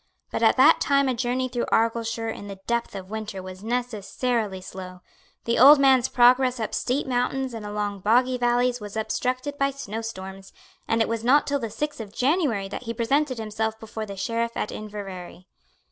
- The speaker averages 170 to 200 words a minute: Yes, average, 190 wpm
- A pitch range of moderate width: Yes, average, 3.3 semitones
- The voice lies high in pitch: Yes, high, 230 Hz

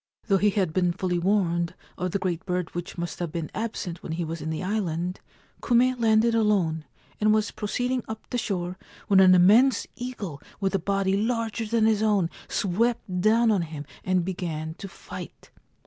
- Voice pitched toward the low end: No, high, 190 Hz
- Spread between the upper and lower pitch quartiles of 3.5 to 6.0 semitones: Yes, average, 3.9 semitones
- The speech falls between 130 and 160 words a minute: No, average, 185 wpm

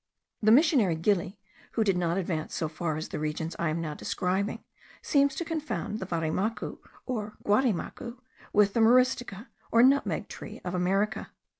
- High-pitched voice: Yes, high, 200 Hz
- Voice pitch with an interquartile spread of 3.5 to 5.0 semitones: No, wide, 5.6 semitones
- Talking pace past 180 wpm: No, average, 160 wpm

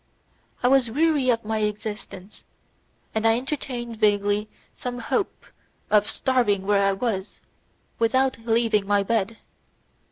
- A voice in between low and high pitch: No, high, 225 Hz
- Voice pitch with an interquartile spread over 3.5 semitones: No, average, 3.2 semitones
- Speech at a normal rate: No, slow, 125 wpm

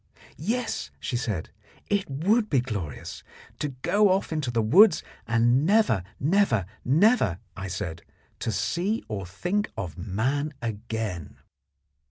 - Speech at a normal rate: No, slow, 125 wpm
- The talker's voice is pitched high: No, low, 125 Hz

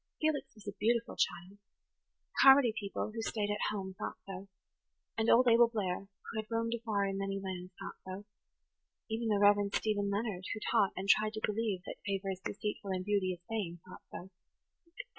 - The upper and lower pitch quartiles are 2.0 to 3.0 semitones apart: Yes, narrow, 2.5 semitones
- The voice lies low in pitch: No, high, 205 Hz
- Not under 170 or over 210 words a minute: Yes, average, 190 wpm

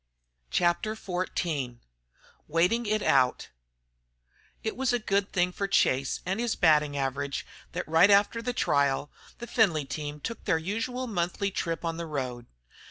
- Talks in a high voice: No, medium, 175 Hz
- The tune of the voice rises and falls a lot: Yes, wide, 6.4 semitones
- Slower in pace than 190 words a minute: Yes, average, 150 wpm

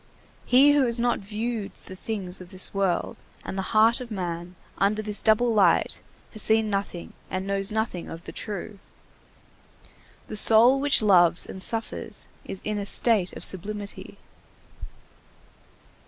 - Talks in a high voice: Yes, high, 210 Hz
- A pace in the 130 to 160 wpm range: Yes, average, 150 wpm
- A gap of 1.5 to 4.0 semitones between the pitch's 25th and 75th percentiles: Yes, average, 2.9 semitones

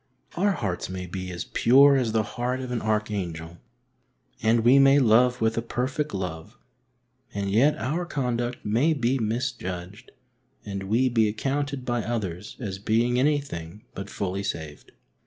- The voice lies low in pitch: Yes, low, 115 Hz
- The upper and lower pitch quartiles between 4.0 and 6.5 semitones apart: Yes, average, 4.7 semitones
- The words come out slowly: No, average, 155 wpm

